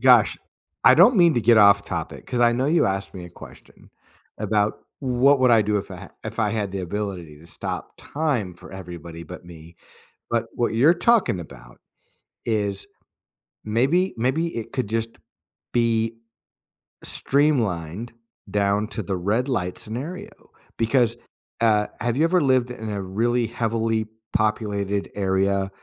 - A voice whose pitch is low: Yes, low, 110 Hz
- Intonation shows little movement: No, average, 3.9 semitones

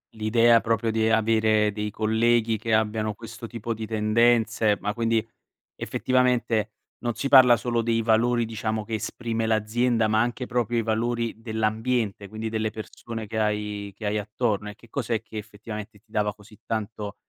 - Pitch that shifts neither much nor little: No, narrow, 1.4 semitones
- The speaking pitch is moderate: No, low, 110 Hz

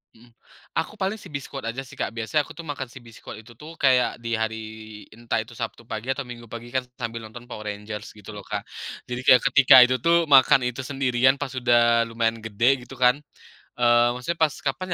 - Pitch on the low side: Yes, low, 120 Hz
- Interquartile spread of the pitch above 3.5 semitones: No, average, 2.8 semitones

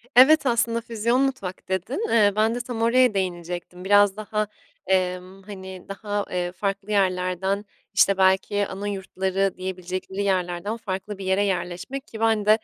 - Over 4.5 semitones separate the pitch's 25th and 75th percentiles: No, narrow, 2.5 semitones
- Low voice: No, high, 195 Hz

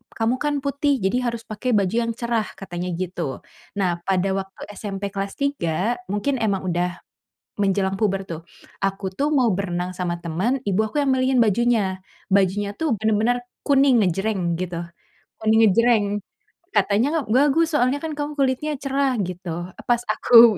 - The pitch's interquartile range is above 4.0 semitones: Yes, average, 5.2 semitones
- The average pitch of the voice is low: No, high, 210 Hz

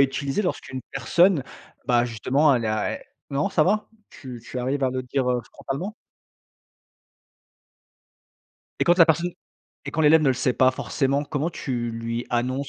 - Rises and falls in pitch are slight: No, average, 3.7 semitones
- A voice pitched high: No, low, 135 Hz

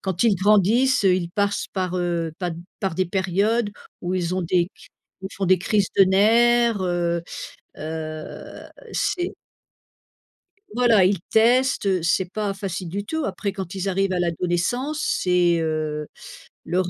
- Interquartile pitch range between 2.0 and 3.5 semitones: Yes, average, 3.2 semitones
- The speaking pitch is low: No, high, 190 Hz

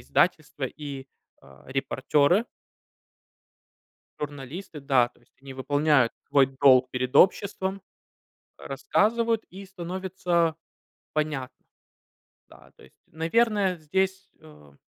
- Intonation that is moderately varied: No, wide, 6.1 semitones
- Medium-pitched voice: Yes, medium, 155 Hz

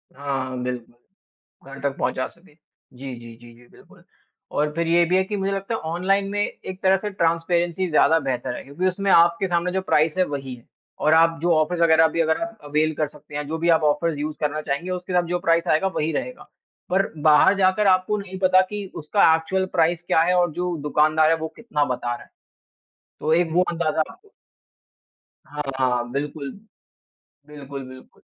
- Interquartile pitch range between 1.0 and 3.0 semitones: No, average, 3.8 semitones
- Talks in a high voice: No, medium, 165 Hz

